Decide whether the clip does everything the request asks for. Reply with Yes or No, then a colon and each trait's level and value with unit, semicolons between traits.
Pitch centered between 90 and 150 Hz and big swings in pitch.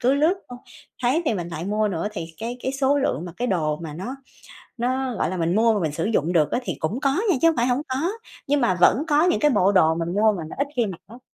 No: high, 220 Hz; wide, 7.3 semitones